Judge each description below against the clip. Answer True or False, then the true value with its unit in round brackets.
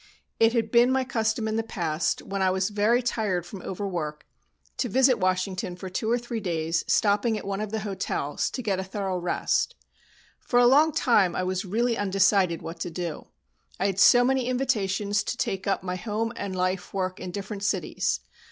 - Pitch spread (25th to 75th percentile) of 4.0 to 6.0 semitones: False (3.6 semitones)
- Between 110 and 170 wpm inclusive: False (200 wpm)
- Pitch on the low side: False (200 Hz)